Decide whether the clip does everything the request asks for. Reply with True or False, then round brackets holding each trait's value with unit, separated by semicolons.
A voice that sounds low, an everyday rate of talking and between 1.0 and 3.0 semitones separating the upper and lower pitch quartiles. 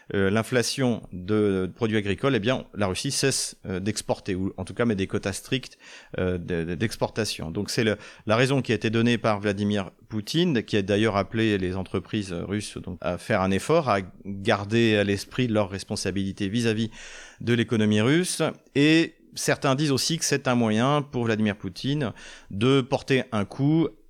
False (110 Hz; 170 wpm; 4.3 semitones)